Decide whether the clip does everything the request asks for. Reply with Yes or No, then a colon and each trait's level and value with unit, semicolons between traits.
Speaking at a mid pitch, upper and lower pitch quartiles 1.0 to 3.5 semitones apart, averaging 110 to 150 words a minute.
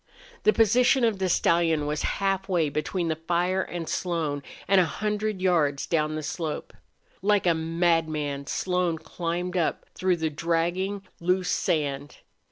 Yes: medium, 170 Hz; average, 3.0 semitones; average, 145 wpm